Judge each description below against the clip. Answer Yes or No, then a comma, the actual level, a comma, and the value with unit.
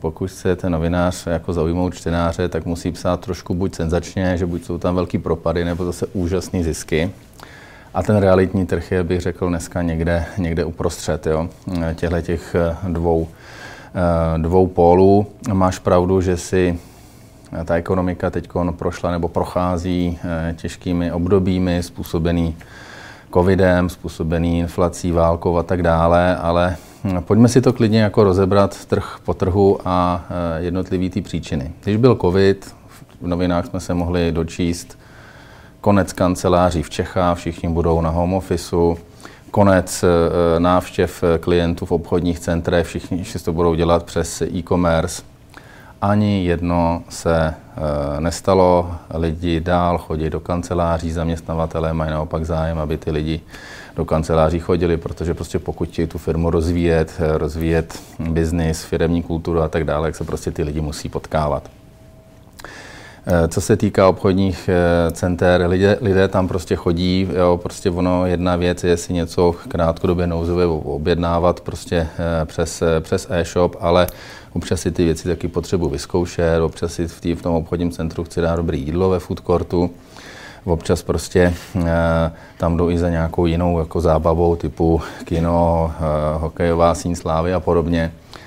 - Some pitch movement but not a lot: No, narrow, 1.5 semitones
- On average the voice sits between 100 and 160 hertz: No, very low, 85 Hz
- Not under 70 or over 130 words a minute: No, average, 140 wpm